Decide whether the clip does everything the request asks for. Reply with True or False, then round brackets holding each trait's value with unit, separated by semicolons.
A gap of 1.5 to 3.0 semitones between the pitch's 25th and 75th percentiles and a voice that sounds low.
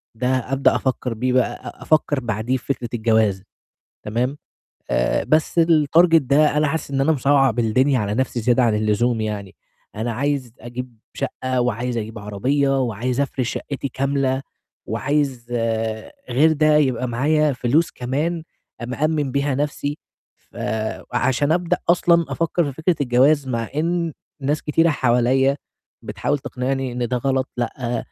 False (3.4 semitones; 130 Hz)